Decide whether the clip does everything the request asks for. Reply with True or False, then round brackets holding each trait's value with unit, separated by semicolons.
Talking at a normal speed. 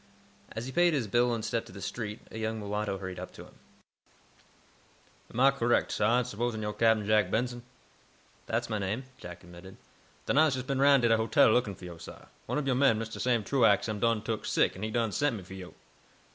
False (230 wpm)